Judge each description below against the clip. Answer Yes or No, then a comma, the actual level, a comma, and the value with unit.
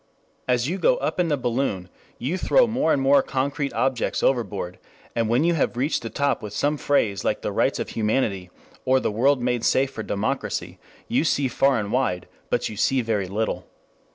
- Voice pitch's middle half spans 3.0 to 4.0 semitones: No, average, 4.4 semitones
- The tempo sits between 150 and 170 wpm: No, average, 200 wpm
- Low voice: Yes, low, 130 Hz